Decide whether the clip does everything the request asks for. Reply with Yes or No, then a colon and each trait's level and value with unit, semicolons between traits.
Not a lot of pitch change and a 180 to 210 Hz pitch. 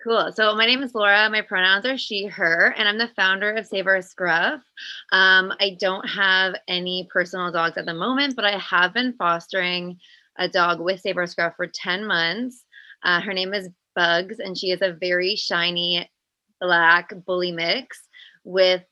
No: average, 3.0 semitones; high, 190 Hz